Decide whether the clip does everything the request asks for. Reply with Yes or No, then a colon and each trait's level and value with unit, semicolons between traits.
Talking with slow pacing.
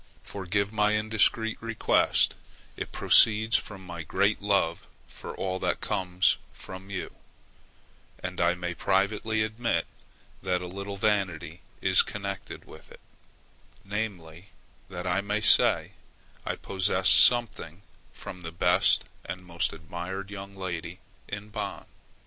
Yes: slow, 125 wpm